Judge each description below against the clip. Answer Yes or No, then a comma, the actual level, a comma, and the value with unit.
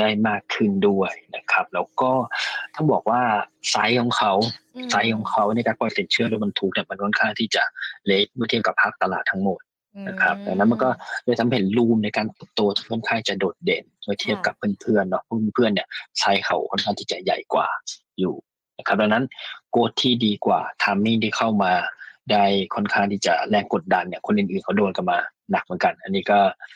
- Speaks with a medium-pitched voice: No, low, 115 Hz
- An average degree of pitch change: Yes, average, 3.4 semitones